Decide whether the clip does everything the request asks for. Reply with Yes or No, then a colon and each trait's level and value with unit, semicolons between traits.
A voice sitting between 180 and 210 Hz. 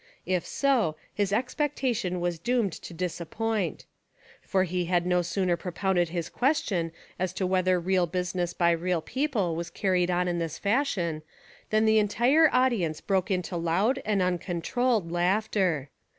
Yes: medium, 185 Hz